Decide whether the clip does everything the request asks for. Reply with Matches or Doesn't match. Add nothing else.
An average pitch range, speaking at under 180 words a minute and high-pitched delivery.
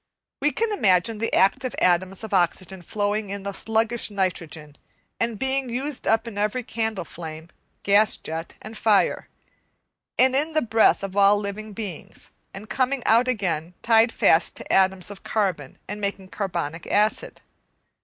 Matches